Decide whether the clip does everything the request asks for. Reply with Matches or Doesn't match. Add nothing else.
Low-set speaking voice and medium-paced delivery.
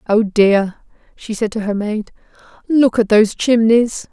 Doesn't match